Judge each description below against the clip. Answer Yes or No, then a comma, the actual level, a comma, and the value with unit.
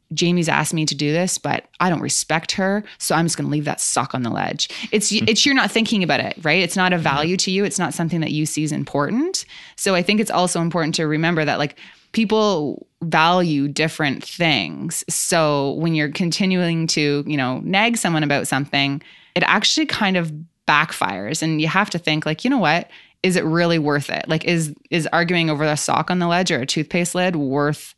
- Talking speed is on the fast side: Yes, fast, 220 wpm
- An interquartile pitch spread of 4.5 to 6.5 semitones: No, average, 3.3 semitones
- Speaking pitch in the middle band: Yes, medium, 165 Hz